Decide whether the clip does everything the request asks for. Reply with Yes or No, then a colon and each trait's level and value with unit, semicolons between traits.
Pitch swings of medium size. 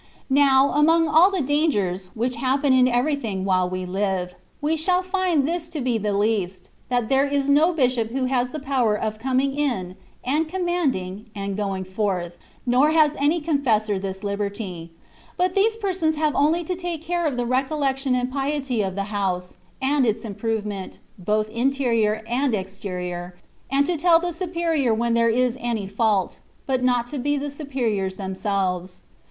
No: wide, 6.4 semitones